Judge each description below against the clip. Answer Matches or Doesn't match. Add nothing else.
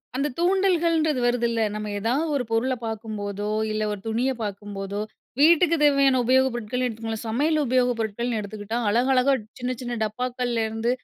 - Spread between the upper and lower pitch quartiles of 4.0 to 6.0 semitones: Doesn't match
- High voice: Matches